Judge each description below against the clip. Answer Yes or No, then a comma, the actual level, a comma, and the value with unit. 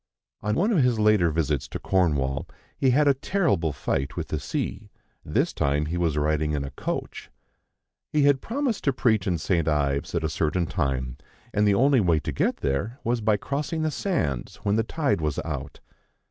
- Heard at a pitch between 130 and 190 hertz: No, very low, 95 Hz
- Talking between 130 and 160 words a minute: No, average, 195 wpm